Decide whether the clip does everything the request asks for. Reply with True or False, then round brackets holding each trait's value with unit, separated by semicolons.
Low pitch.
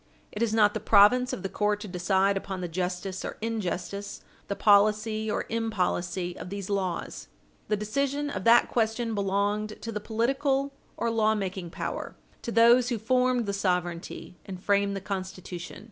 False (205 Hz)